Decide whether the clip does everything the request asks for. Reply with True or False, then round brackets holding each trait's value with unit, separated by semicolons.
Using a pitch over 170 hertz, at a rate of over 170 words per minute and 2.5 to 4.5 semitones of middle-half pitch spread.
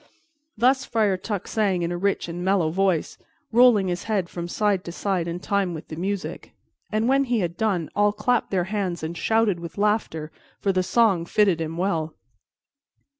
True (190 Hz; 185 wpm; 3.5 semitones)